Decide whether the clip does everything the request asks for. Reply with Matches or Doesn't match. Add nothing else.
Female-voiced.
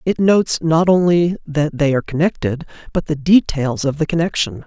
Doesn't match